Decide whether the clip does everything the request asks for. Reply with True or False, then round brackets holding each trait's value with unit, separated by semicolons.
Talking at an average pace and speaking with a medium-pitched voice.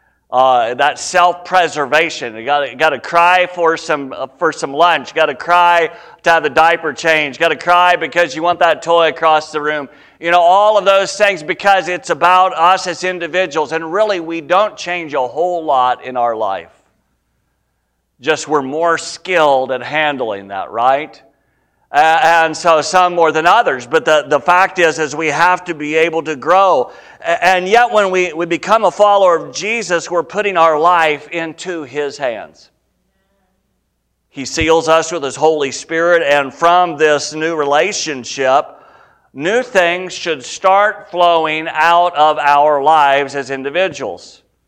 True (165 wpm; 165 Hz)